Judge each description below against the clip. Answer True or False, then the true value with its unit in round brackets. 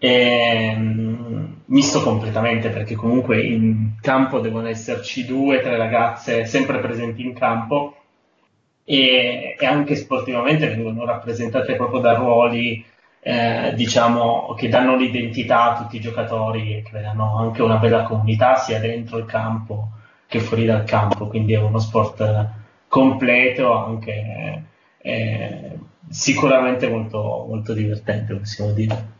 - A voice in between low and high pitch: False (115 Hz)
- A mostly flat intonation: True (2.2 semitones)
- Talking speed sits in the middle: True (130 wpm)